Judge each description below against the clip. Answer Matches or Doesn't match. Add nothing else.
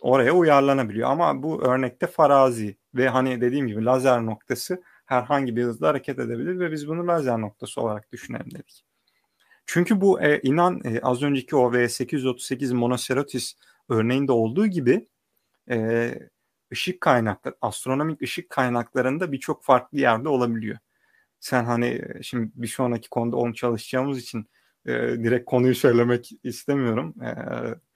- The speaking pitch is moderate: Doesn't match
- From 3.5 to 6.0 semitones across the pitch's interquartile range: Doesn't match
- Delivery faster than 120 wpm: Matches